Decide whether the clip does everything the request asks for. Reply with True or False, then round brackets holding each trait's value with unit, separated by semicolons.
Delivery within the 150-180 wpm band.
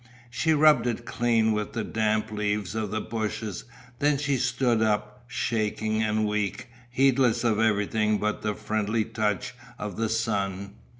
True (155 wpm)